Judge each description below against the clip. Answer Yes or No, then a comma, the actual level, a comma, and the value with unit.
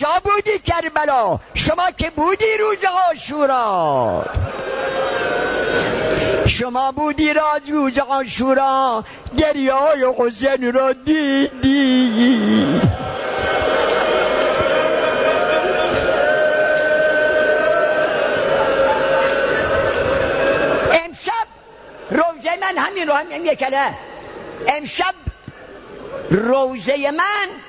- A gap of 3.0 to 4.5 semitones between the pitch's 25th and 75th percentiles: No, wide, 5.5 semitones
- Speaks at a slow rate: Yes, slow, 65 wpm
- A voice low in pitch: No, very high, 305 Hz